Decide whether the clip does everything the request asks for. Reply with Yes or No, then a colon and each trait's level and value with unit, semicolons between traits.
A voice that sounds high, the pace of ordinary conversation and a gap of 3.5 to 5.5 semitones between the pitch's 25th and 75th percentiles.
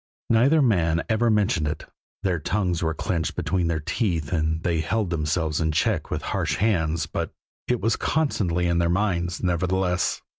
No: very low, 90 Hz; average, 170 wpm; average, 4.2 semitones